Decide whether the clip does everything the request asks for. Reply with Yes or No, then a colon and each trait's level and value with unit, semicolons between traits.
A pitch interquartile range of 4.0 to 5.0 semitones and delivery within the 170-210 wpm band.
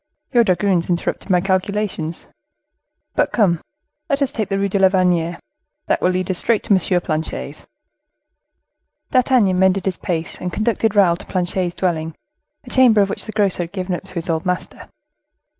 No: average, 2.7 semitones; average, 175 wpm